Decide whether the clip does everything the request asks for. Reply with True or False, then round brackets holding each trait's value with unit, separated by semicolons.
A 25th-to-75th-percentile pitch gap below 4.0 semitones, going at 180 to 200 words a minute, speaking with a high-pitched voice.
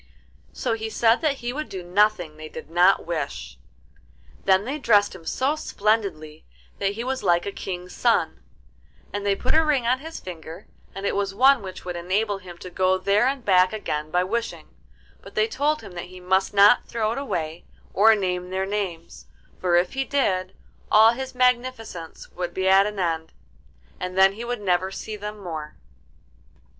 False (4.4 semitones; 190 wpm; 195 Hz)